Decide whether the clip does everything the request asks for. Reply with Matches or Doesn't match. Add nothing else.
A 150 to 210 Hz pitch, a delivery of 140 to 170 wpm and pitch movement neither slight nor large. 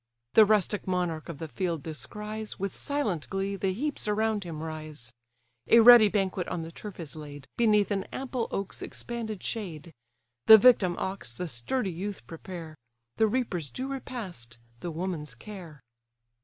Matches